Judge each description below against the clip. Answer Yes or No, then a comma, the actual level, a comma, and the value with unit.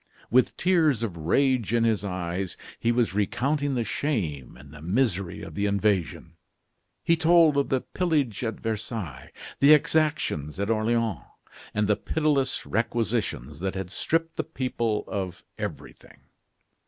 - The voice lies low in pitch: Yes, low, 115 Hz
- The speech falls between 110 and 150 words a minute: Yes, average, 140 wpm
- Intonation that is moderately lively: No, wide, 6.4 semitones